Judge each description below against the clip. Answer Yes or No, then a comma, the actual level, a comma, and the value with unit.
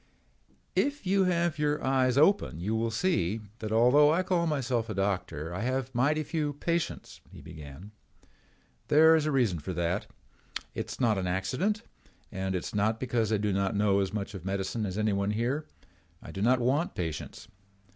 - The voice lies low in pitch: Yes, low, 115 Hz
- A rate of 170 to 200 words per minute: Yes, average, 185 wpm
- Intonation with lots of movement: Yes, wide, 7.2 semitones